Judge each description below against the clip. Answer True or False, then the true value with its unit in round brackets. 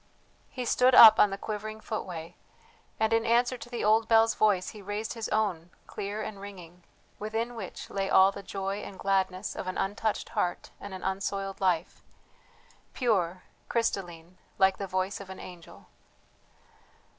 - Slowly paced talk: False (160 wpm)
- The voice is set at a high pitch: True (200 Hz)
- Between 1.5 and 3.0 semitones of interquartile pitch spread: True (2.7 semitones)